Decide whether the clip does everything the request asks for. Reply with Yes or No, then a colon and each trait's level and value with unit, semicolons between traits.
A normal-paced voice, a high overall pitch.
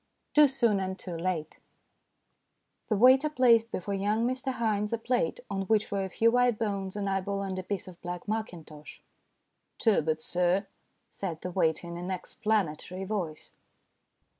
Yes: average, 165 wpm; high, 195 Hz